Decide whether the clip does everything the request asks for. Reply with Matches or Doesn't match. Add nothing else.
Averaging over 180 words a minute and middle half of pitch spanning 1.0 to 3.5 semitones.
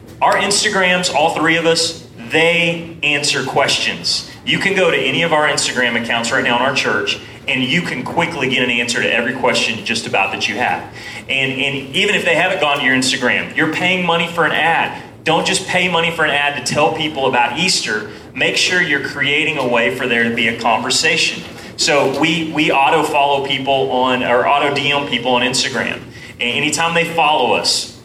Doesn't match